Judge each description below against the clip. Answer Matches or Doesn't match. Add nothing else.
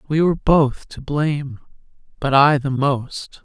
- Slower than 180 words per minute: Matches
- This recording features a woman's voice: Matches